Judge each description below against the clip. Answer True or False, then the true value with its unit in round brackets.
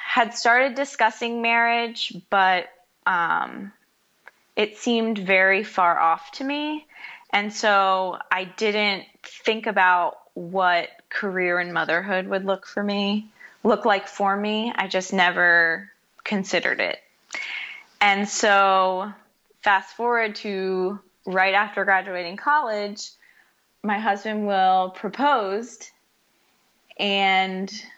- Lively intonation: False (2.9 semitones)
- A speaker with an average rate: False (105 wpm)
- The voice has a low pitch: False (200 Hz)